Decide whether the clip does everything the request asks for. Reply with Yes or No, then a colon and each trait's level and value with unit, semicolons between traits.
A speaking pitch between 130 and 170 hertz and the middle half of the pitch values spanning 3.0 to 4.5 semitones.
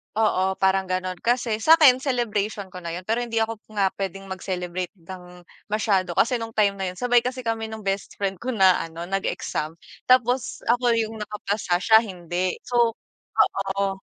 No: high, 200 Hz; average, 3.6 semitones